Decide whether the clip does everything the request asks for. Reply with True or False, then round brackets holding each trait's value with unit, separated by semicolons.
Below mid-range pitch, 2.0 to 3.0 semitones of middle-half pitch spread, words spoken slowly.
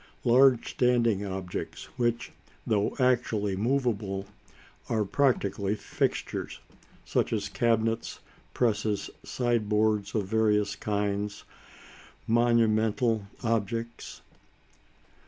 True (110 Hz; 2.4 semitones; 80 wpm)